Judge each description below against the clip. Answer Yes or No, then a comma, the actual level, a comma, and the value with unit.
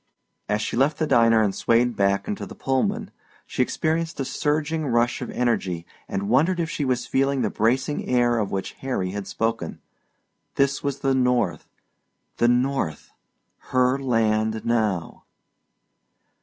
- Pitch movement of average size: Yes, average, 3.9 semitones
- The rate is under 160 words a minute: Yes, average, 150 wpm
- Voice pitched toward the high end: No, low, 125 Hz